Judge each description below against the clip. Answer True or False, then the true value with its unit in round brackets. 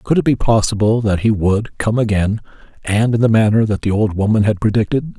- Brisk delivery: True (220 wpm)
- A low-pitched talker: True (110 Hz)